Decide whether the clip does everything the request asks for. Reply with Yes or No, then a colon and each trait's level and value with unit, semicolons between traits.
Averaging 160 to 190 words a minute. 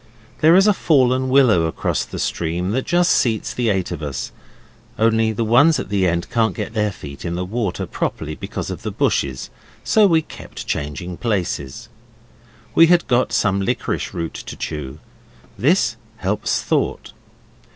Yes: average, 165 wpm